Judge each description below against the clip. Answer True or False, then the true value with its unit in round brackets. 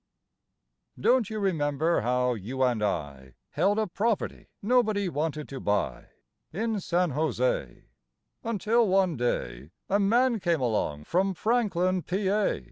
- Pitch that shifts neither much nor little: False (8.4 semitones)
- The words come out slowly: True (125 wpm)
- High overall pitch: False (180 Hz)